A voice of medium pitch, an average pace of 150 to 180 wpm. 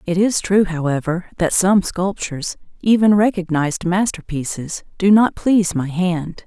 No: medium, 180 Hz; average, 140 wpm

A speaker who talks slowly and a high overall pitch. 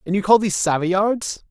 No: average, 200 wpm; high, 195 Hz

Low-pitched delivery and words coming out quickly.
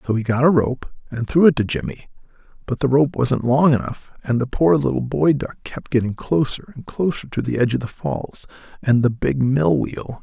Yes: low, 130 Hz; fast, 215 wpm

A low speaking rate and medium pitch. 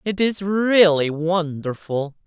Yes: slow, 105 wpm; medium, 175 Hz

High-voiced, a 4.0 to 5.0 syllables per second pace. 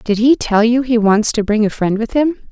No: high, 230 Hz; 5.2 syllables/s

